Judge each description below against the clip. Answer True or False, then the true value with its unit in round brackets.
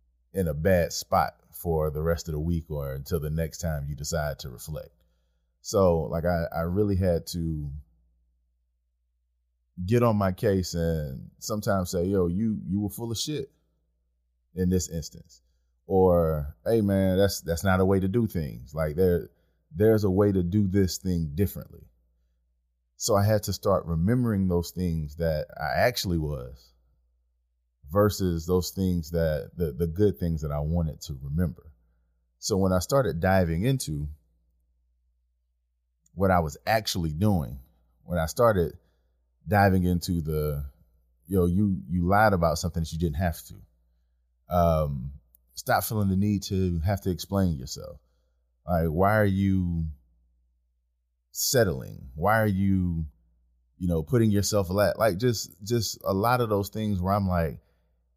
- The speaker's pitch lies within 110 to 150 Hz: False (85 Hz)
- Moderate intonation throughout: False (7.2 semitones)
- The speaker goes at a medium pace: True (160 wpm)